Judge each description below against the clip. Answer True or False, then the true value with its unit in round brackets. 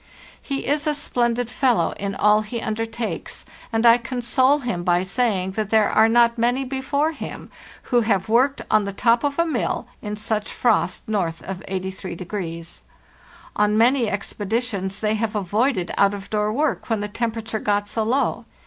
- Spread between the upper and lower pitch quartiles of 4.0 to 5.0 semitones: False (3.2 semitones)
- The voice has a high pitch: True (220 Hz)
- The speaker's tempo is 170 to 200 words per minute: True (175 wpm)